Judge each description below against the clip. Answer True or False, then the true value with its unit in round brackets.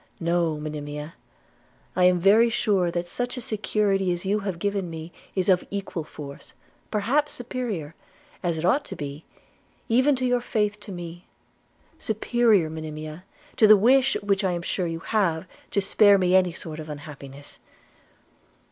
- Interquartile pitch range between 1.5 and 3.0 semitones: False (4.7 semitones)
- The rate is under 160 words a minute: False (165 wpm)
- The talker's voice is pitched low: False (185 Hz)